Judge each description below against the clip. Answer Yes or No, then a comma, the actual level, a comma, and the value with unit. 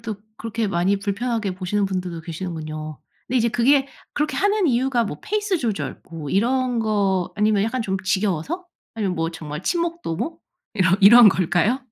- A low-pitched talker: No, high, 210 Hz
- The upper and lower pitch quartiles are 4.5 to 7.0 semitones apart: Yes, wide, 5.4 semitones